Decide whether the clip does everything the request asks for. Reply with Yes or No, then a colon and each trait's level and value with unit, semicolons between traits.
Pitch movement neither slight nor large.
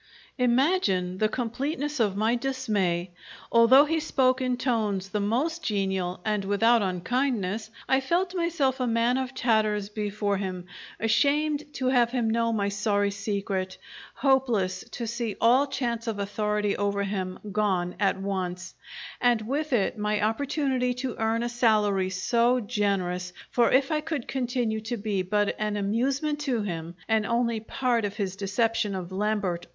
Yes: average, 4.1 semitones